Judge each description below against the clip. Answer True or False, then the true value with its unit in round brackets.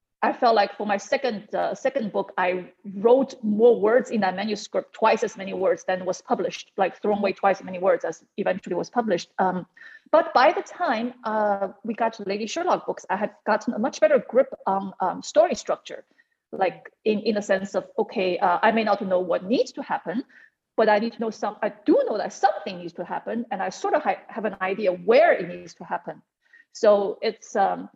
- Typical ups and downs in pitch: True (4.3 semitones)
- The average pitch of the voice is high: True (215 Hz)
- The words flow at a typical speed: False (220 wpm)